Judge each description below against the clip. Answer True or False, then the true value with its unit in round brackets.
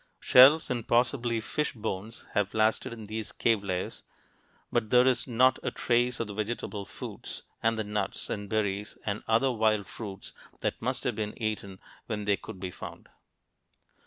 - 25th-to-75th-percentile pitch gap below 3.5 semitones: True (2.6 semitones)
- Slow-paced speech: False (170 wpm)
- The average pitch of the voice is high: False (110 Hz)